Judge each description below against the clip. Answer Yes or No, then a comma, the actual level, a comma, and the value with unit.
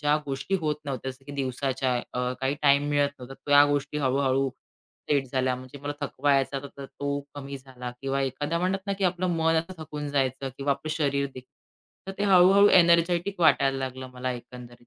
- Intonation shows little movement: Yes, narrow, 2.3 semitones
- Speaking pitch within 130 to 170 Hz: Yes, medium, 140 Hz